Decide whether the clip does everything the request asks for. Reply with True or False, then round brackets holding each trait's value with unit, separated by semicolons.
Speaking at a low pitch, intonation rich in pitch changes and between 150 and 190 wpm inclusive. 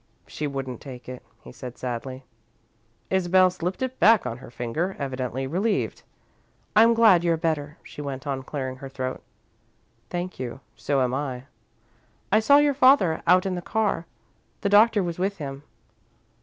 False (155 Hz; 6.5 semitones; 160 wpm)